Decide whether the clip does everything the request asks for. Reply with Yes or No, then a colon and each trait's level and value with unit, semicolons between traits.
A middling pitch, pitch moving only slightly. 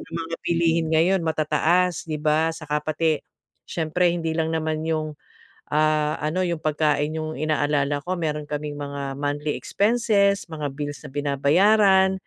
Yes: medium, 155 Hz; narrow, 2.3 semitones